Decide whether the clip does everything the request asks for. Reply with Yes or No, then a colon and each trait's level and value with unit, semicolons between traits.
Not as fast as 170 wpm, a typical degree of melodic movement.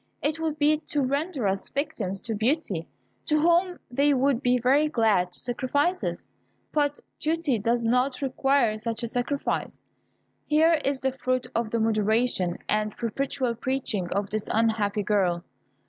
Yes: average, 155 wpm; average, 5.0 semitones